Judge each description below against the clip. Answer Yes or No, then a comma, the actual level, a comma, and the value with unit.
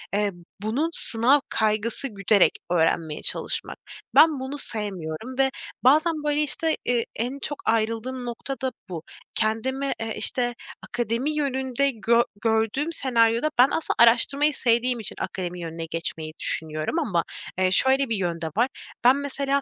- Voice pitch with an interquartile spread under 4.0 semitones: No, average, 4.7 semitones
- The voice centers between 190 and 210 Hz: No, high, 235 Hz